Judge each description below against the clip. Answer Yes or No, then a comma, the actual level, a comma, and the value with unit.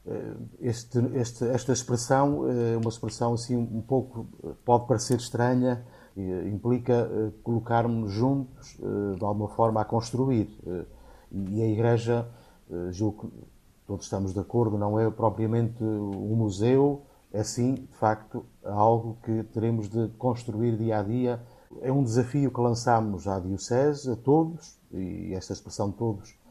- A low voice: Yes, low, 115 Hz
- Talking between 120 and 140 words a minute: Yes, average, 135 wpm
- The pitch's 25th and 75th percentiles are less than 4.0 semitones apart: Yes, narrow, 2.5 semitones